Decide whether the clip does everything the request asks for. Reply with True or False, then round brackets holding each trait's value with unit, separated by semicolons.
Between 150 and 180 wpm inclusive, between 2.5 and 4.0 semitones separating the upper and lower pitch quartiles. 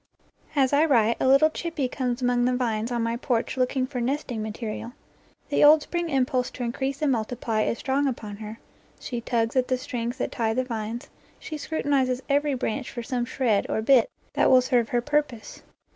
False (195 wpm; 2.8 semitones)